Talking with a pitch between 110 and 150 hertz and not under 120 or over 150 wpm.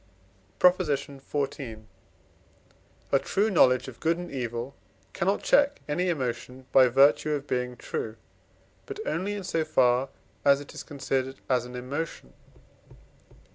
Yes: medium, 140 Hz; slow, 135 wpm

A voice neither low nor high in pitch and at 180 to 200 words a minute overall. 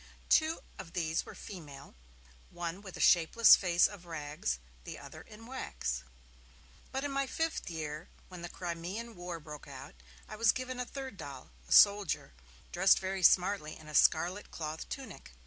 No: medium, 175 Hz; average, 165 wpm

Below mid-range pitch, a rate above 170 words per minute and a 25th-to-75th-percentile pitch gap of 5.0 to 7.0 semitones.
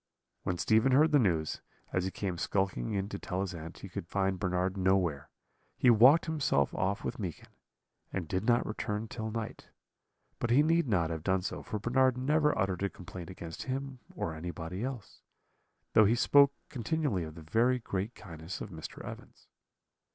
Yes: low, 100 Hz; average, 180 wpm; wide, 5.5 semitones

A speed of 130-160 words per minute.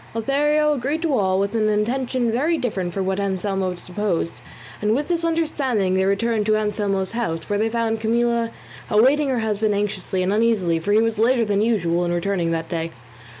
No: average, 190 wpm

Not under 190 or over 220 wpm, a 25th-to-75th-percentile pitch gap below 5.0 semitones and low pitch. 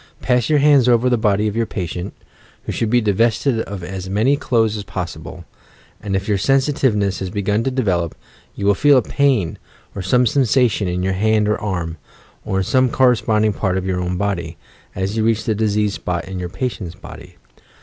Yes: average, 200 wpm; average, 4.1 semitones; low, 105 Hz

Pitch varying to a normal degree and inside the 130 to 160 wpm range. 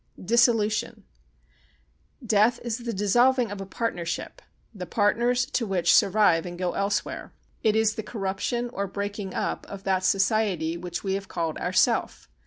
Yes: average, 3.2 semitones; average, 150 wpm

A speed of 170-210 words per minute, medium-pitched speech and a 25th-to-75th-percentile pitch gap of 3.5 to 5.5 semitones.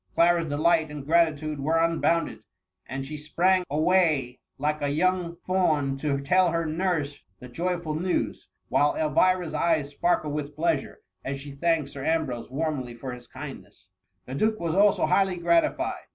No: average, 175 wpm; medium, 155 Hz; average, 3.1 semitones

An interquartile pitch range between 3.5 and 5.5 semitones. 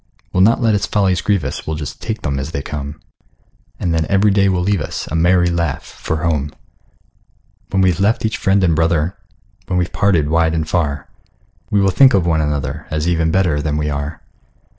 Yes: average, 4.1 semitones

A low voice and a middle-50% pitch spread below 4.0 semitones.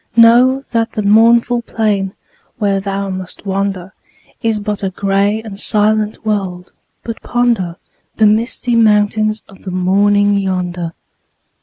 No: high, 205 Hz; narrow, 2.4 semitones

